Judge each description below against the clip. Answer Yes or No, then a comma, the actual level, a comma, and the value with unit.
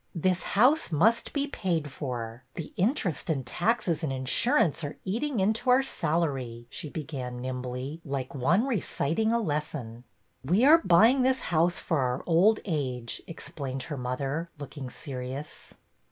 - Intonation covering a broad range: Yes, wide, 7.2 semitones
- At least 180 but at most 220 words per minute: No, average, 145 wpm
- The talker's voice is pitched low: No, medium, 155 Hz